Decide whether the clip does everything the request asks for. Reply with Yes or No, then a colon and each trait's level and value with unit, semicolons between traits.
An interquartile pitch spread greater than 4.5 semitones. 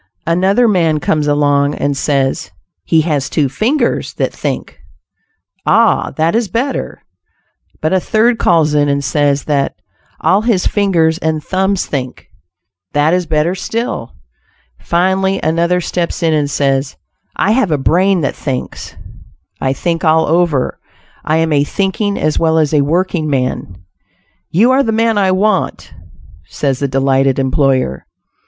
Yes: average, 4.9 semitones